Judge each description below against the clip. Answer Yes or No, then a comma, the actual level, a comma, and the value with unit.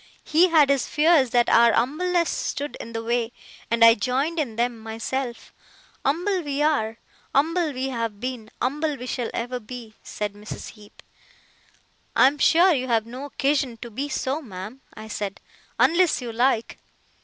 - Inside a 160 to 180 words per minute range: Yes, average, 165 wpm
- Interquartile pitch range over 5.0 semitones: No, average, 4.3 semitones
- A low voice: No, very high, 255 Hz